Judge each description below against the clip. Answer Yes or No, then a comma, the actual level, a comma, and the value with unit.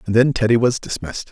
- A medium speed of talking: No, fast, 230 wpm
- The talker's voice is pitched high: No, low, 115 Hz